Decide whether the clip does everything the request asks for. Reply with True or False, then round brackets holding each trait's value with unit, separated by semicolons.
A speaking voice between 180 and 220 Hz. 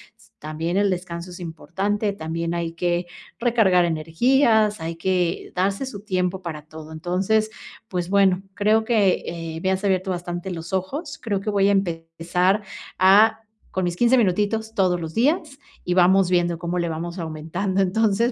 True (185 Hz)